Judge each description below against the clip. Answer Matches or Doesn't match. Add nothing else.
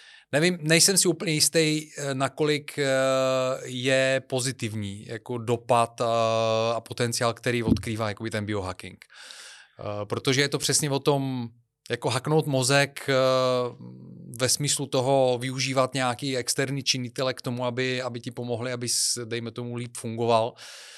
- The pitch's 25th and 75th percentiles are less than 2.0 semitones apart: Doesn't match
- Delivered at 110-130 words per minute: Matches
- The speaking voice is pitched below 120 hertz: Doesn't match